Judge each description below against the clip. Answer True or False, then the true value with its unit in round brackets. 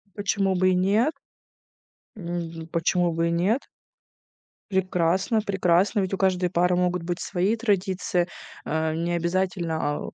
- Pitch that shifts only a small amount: True (2.1 semitones)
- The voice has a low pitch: False (180 Hz)